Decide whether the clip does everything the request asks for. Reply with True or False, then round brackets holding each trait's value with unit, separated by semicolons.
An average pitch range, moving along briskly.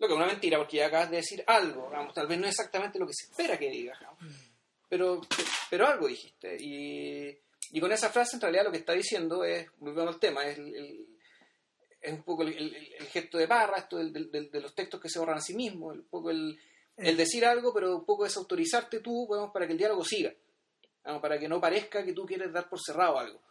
False (7.3 semitones; 245 wpm)